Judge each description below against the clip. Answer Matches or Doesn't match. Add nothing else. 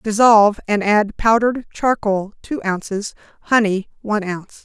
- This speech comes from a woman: Matches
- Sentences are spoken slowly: Matches